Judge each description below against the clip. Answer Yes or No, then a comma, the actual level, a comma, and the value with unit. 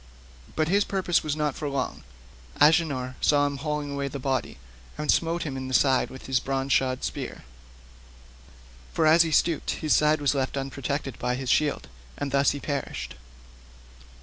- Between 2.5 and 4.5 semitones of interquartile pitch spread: Yes, average, 3.4 semitones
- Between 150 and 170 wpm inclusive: Yes, average, 165 wpm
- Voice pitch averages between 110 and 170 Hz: Yes, medium, 140 Hz